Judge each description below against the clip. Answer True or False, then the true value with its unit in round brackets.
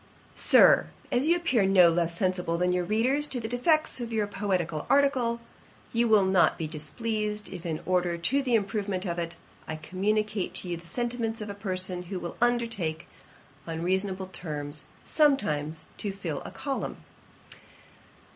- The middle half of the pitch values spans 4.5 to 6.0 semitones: True (5.1 semitones)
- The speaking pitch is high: True (195 Hz)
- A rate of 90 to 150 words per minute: False (165 wpm)